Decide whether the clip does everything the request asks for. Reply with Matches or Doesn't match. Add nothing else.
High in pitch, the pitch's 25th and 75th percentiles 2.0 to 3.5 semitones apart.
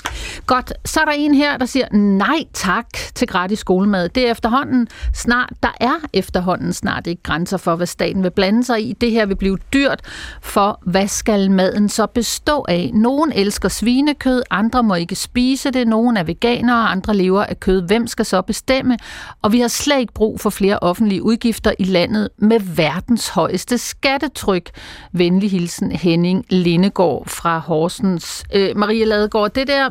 Doesn't match